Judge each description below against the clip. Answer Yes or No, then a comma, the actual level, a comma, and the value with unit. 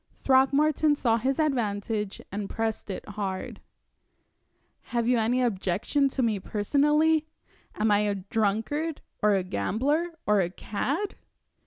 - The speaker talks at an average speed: No, slow, 130 wpm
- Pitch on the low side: No, high, 225 Hz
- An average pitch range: No, wide, 5.7 semitones